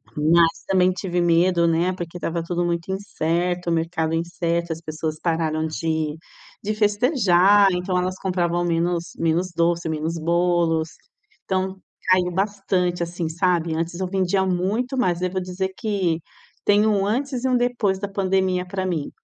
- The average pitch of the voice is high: No, medium, 180 Hz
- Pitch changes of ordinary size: No, narrow, 2.3 semitones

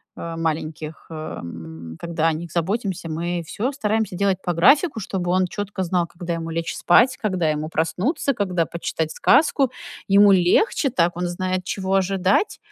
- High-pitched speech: No, medium, 180 Hz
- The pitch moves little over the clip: No, average, 3.4 semitones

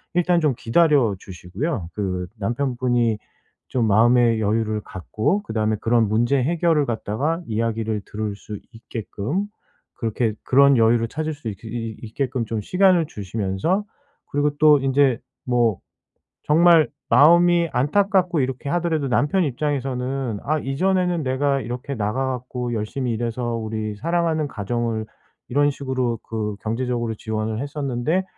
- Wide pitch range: No, average, 4.9 semitones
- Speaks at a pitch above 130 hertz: No, low, 125 Hz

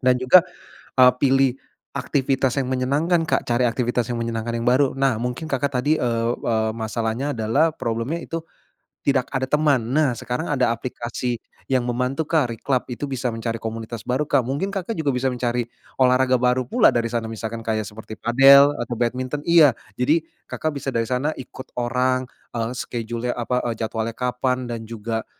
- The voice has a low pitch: Yes, low, 125 Hz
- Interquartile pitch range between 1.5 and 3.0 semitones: Yes, average, 2.7 semitones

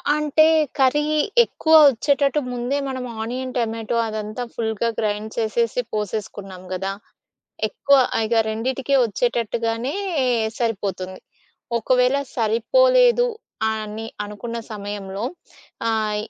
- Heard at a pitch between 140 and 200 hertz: No, high, 230 Hz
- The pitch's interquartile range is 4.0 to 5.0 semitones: No, average, 3.3 semitones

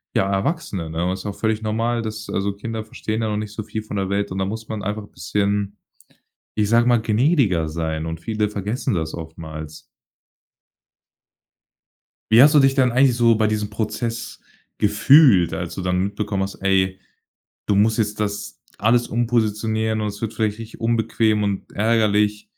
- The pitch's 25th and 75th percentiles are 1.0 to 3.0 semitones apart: Yes, narrow, 2.4 semitones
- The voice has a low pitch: Yes, low, 105 Hz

